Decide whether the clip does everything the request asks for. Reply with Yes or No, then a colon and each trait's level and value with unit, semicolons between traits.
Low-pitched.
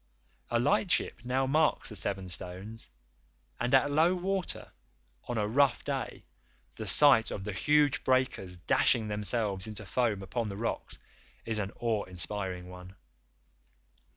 Yes: low, 110 Hz